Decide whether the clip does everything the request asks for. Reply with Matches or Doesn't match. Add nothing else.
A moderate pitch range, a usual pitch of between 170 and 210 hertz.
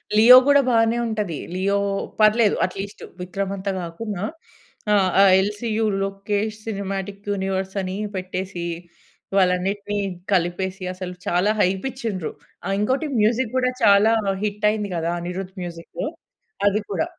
Doesn't match